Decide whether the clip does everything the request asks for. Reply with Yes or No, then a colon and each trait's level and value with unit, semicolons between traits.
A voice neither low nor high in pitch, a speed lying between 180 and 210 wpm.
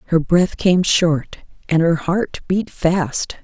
No: medium, 170 Hz; average, 155 wpm